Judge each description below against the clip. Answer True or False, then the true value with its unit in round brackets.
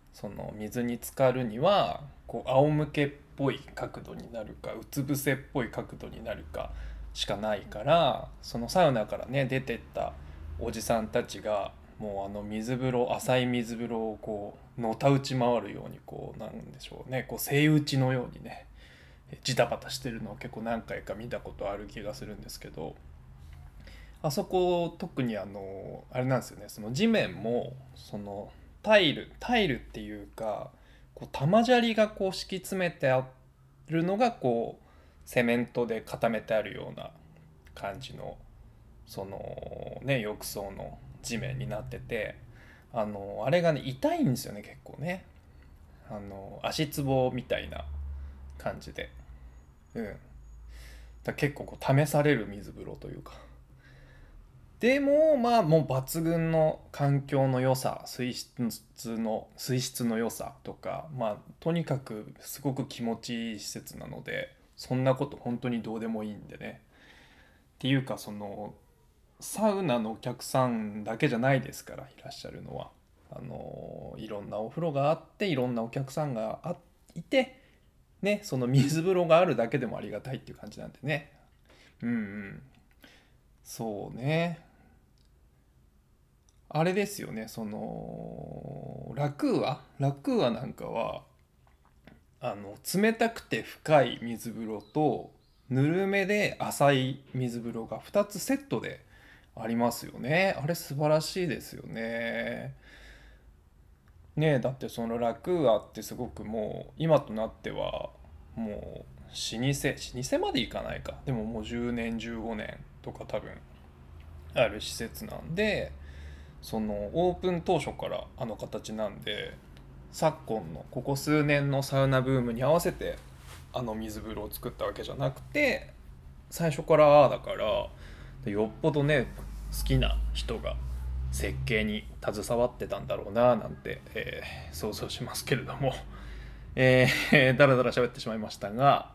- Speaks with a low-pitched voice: True (120 Hz)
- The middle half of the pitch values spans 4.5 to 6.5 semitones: True (5.9 semitones)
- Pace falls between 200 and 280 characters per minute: True (275 characters per minute)